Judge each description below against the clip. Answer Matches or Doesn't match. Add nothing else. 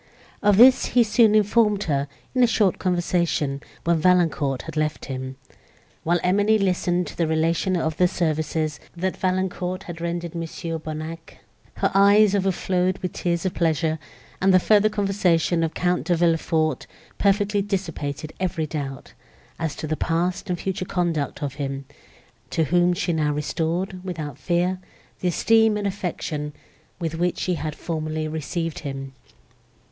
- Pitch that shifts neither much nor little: Matches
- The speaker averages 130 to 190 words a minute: Matches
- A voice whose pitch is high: Doesn't match